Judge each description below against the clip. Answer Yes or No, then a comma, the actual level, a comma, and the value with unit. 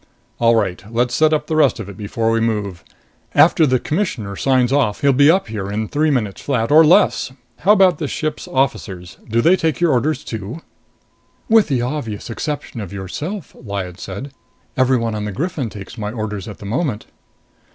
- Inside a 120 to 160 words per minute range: No, average, 190 wpm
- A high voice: No, low, 120 Hz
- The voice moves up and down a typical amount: No, wide, 6.3 semitones